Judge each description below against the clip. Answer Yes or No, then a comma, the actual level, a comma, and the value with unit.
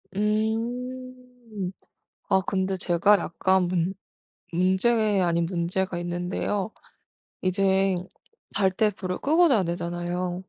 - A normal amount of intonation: Yes, average, 3.2 semitones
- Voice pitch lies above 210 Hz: No, high, 190 Hz